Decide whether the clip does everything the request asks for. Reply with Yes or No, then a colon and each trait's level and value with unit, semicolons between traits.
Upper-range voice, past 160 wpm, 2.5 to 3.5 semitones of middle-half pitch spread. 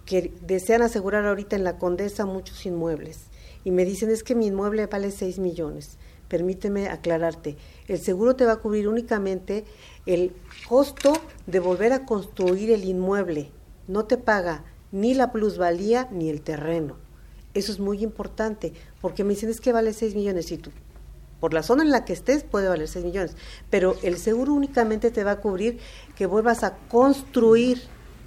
No: high, 200 Hz; average, 175 wpm; average, 4.1 semitones